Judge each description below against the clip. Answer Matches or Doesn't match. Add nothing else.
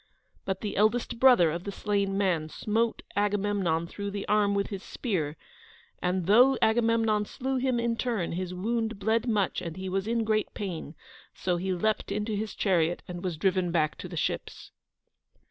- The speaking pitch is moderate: Doesn't match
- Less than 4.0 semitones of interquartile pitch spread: Matches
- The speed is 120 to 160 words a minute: Doesn't match